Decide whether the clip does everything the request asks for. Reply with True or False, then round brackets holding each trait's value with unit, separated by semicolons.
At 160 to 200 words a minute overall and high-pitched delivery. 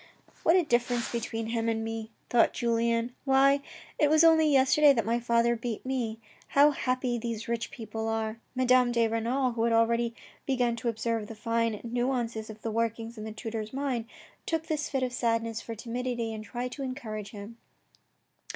True (180 wpm; 235 Hz)